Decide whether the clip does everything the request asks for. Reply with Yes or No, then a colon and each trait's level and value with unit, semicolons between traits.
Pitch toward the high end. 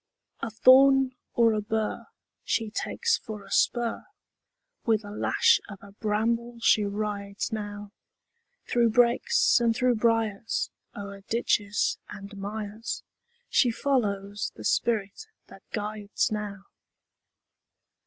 Yes: high, 215 Hz